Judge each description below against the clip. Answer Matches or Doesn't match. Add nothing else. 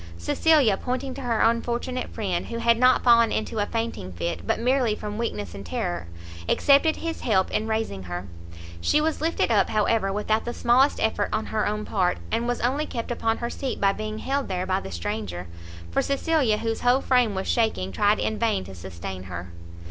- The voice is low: Doesn't match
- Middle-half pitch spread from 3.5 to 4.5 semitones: Doesn't match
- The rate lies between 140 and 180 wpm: Doesn't match